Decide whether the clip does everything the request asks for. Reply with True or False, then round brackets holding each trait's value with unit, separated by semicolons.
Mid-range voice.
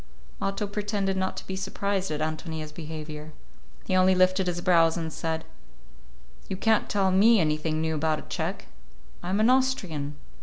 True (180 Hz)